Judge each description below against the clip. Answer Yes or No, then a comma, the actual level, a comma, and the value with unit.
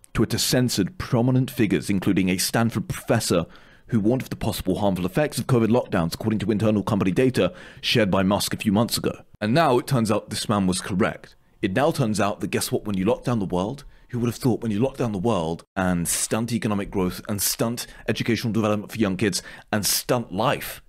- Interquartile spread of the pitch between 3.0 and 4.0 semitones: Yes, average, 3.4 semitones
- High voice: No, low, 110 Hz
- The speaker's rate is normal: No, fast, 220 wpm